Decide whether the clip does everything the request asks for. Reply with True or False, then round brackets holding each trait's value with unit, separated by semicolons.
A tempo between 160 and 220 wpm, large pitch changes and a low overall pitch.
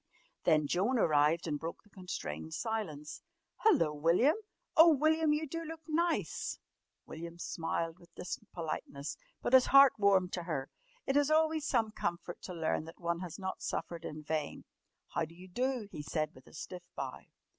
False (170 wpm; 8.6 semitones; 175 Hz)